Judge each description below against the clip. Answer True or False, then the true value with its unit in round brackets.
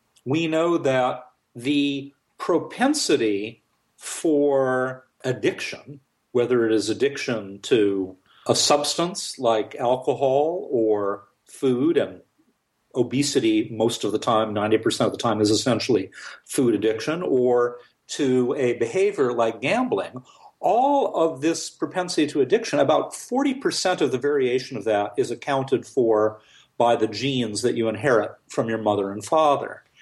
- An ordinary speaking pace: False (130 wpm)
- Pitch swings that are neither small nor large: False (6.0 semitones)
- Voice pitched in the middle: False (130 Hz)